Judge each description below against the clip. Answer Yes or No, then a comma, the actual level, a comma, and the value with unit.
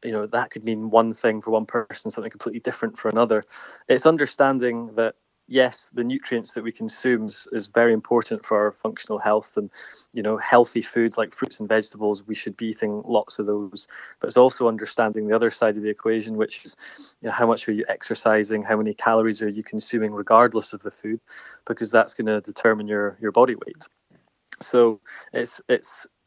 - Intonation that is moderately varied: No, narrow, 1.4 semitones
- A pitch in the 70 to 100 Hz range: No, low, 110 Hz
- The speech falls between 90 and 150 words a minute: No, average, 200 wpm